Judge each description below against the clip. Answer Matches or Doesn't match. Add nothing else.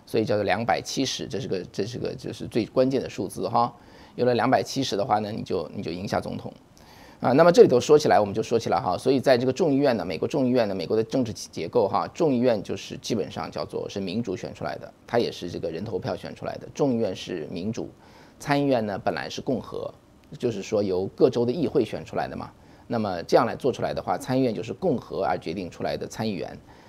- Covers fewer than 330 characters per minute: Doesn't match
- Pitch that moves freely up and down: Doesn't match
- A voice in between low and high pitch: Doesn't match